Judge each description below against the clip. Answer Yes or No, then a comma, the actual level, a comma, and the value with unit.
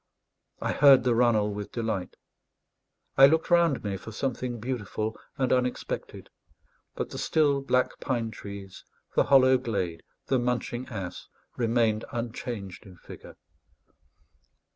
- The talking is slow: Yes, slow, 125 wpm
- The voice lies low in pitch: Yes, low, 120 Hz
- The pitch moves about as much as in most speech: Yes, average, 3.7 semitones